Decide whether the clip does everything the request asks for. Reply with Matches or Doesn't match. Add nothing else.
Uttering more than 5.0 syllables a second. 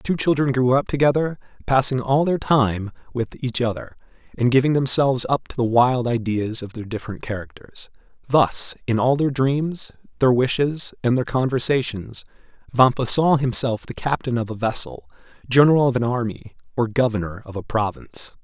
Matches